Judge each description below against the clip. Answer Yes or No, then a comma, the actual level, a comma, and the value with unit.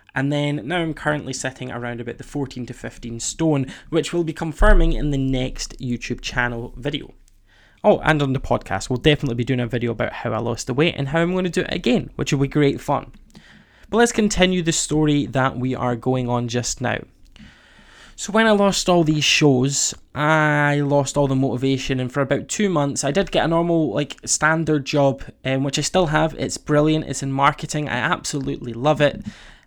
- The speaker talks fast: Yes, fast, 210 wpm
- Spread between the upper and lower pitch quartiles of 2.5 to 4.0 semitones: Yes, average, 3.5 semitones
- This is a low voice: No, medium, 145 Hz